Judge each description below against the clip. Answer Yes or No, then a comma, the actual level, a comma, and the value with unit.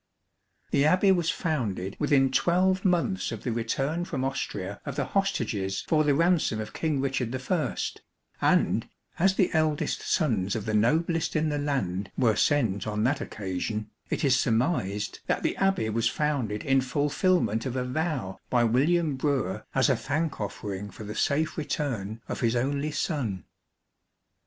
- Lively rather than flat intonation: Yes, wide, 6.2 semitones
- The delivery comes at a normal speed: Yes, average, 160 wpm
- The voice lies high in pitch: No, low, 135 Hz